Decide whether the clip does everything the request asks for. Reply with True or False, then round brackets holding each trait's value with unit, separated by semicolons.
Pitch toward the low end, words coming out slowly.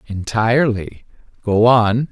True (110 Hz; 85 wpm)